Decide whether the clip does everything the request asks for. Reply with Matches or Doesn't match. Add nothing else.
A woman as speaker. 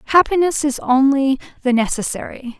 Matches